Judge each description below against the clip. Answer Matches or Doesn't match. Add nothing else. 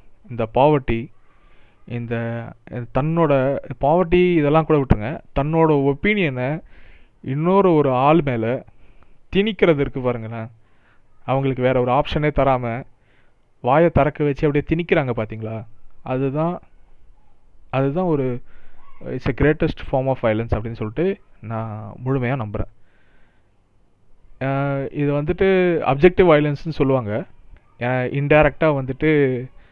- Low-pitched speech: Matches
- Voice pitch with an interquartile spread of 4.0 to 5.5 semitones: Matches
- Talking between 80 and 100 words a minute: Matches